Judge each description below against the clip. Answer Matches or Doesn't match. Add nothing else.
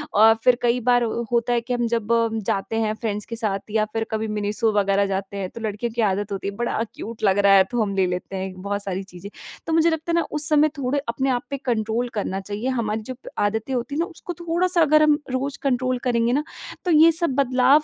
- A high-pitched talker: Matches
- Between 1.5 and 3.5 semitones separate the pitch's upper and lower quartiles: Doesn't match